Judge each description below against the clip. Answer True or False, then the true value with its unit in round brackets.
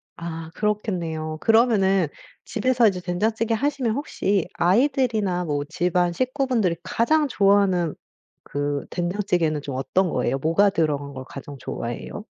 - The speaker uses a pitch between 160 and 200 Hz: True (185 Hz)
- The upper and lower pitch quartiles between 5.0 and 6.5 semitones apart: True (5.6 semitones)